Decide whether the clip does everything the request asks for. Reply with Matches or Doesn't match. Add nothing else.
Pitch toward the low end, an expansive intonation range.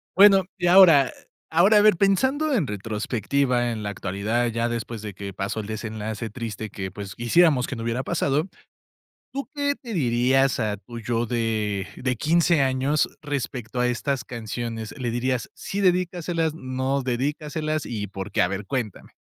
Matches